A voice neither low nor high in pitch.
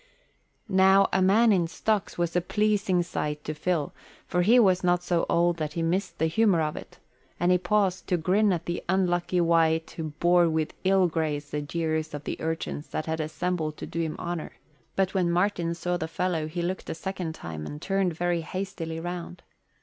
Yes: medium, 175 Hz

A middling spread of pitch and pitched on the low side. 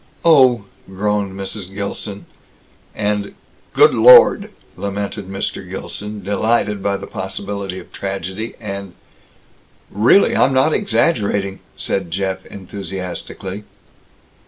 No: narrow, 1.7 semitones; low, 100 Hz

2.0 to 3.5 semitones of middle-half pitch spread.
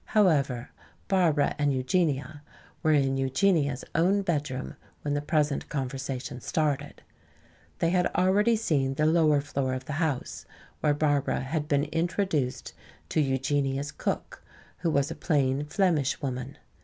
Yes: average, 3.2 semitones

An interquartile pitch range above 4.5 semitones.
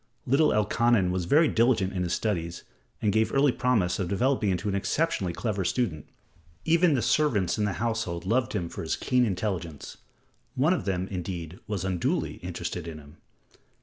Yes: wide, 5.4 semitones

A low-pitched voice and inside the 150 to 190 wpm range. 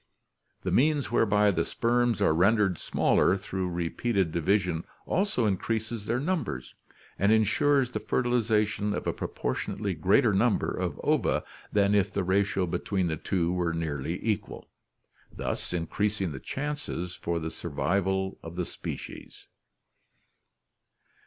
No: low, 100 Hz; average, 140 wpm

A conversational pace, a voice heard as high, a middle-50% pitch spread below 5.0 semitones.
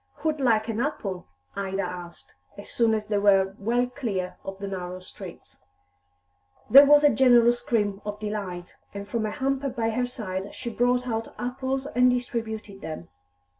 Yes: average, 170 wpm; high, 220 Hz; average, 4.0 semitones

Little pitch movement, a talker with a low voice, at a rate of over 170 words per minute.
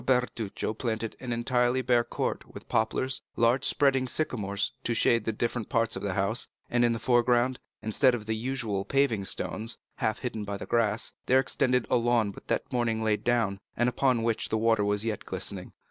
Yes: narrow, 2.3 semitones; low, 115 Hz; average, 190 wpm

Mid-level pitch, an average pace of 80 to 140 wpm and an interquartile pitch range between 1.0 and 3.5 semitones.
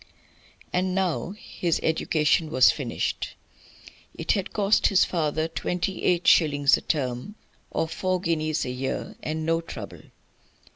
Yes: medium, 165 Hz; slow, 135 wpm; average, 3.0 semitones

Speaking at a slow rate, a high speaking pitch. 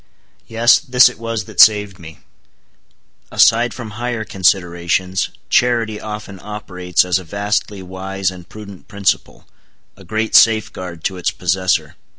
No: slow, 130 wpm; low, 100 Hz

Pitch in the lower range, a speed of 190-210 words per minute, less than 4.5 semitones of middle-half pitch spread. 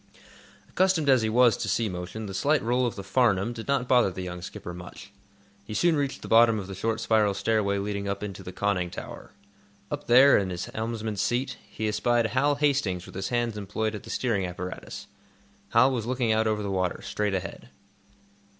Yes: low, 110 Hz; fast, 205 wpm; average, 3.7 semitones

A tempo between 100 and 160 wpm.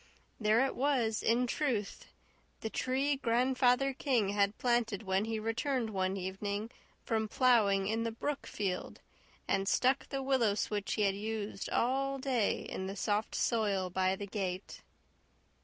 Yes: average, 150 wpm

